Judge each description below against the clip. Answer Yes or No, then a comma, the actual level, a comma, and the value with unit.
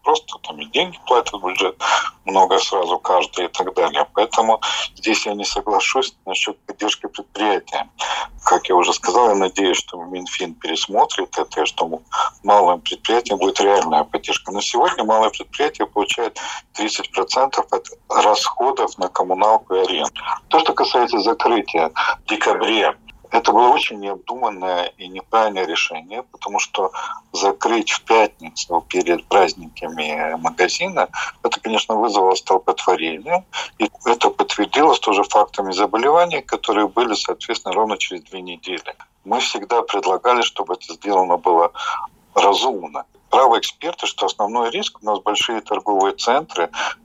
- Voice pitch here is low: No, medium, 175 Hz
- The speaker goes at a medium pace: Yes, average, 135 wpm